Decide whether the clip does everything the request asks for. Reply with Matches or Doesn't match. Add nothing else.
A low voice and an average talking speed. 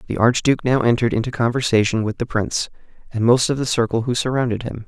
Doesn't match